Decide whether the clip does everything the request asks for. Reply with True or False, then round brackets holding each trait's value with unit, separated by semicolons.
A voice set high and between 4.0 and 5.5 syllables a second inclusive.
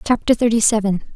False (220 Hz; 6.3 syllables/s)